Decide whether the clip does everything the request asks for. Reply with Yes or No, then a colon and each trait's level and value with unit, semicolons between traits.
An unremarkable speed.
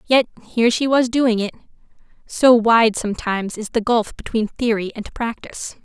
Yes: average, 165 wpm